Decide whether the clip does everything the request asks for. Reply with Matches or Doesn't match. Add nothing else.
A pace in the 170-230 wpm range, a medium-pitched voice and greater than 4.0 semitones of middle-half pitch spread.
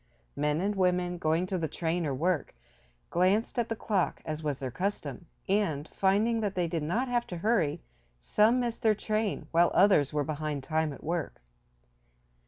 Matches